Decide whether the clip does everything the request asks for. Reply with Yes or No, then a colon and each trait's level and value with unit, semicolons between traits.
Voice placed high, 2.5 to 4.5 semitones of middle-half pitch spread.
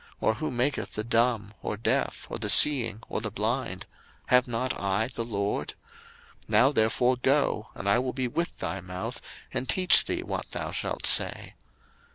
No: low, 115 Hz; average, 3.3 semitones